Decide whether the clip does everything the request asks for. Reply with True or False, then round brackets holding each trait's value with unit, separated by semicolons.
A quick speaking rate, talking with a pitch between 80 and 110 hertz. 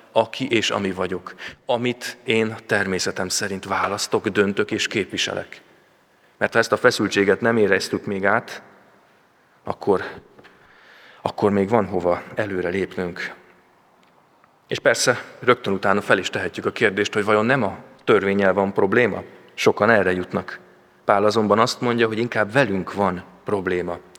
False (140 wpm; 105 Hz)